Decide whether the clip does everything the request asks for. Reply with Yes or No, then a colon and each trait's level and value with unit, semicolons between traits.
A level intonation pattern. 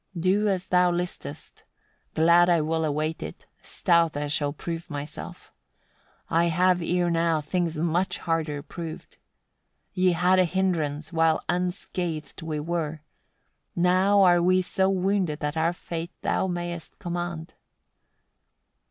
Yes: narrow, 2.0 semitones